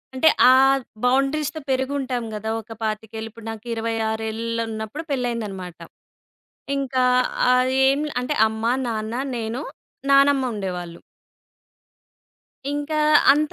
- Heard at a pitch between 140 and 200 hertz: No, high, 230 Hz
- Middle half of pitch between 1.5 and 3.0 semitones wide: No, average, 3.7 semitones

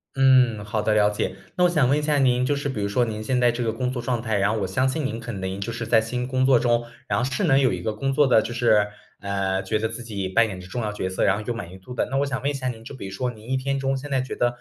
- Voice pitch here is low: Yes, low, 120 Hz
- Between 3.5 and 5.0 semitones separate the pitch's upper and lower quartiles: Yes, average, 3.8 semitones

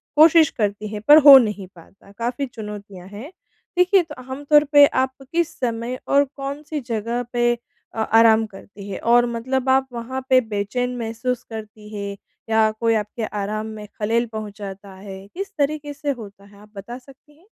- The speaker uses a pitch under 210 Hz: No, high, 230 Hz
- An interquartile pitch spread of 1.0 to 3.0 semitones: No, average, 4.7 semitones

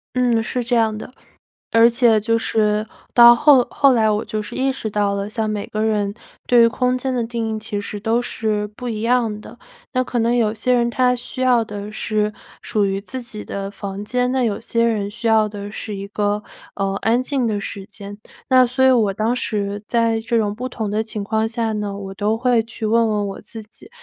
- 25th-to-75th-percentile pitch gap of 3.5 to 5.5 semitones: No, narrow, 2.4 semitones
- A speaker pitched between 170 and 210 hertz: No, high, 220 Hz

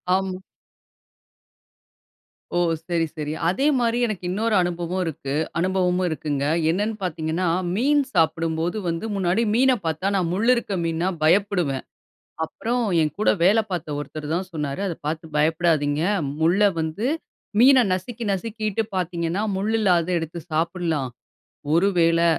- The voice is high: No, medium, 175 Hz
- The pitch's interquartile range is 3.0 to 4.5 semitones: Yes, average, 3.8 semitones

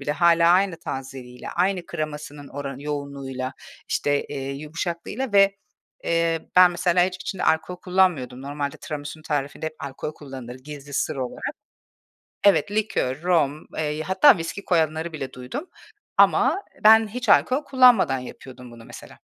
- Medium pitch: Yes, medium, 155 Hz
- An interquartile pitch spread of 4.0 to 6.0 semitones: Yes, average, 4.7 semitones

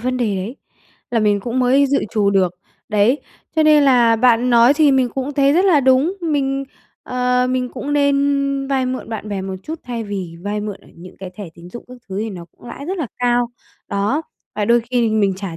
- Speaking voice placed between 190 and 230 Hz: No, high, 245 Hz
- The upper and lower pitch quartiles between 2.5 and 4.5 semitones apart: No, average, 4.9 semitones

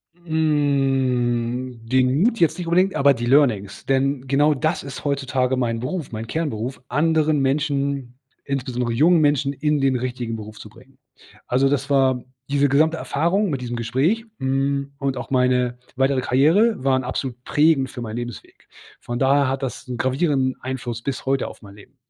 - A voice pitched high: No, low, 135 Hz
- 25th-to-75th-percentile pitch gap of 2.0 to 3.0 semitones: Yes, narrow, 2.6 semitones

